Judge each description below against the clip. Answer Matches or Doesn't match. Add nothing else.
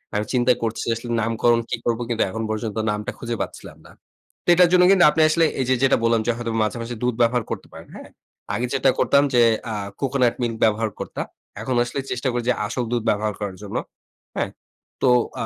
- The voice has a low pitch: Matches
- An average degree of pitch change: Doesn't match